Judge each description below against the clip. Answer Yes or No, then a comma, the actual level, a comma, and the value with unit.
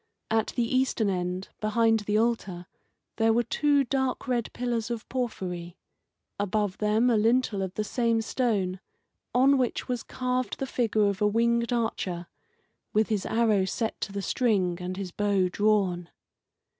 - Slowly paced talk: No, average, 155 wpm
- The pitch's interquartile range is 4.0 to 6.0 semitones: No, average, 3.4 semitones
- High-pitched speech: Yes, high, 220 Hz